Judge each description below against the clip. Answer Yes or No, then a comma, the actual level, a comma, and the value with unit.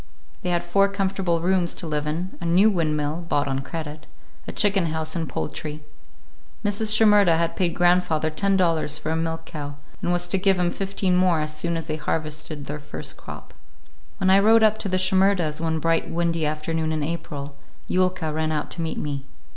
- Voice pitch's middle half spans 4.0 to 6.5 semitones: No, average, 3.2 semitones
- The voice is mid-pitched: Yes, medium, 165 Hz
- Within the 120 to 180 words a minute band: No, average, 190 wpm